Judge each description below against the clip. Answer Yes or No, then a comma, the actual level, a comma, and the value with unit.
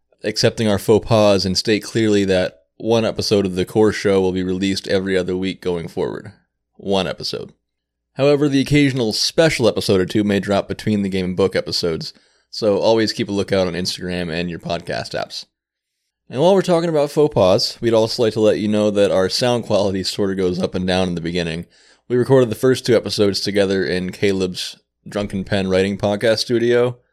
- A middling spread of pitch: Yes, average, 3.4 semitones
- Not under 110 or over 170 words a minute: No, average, 200 wpm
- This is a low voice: Yes, low, 100 Hz